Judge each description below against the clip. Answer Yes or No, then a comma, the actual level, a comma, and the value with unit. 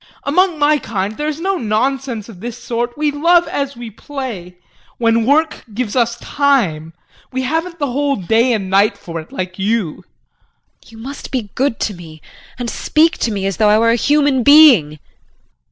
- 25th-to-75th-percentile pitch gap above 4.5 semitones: Yes, wide, 5.6 semitones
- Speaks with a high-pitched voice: Yes, high, 240 Hz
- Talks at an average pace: Yes, average, 185 wpm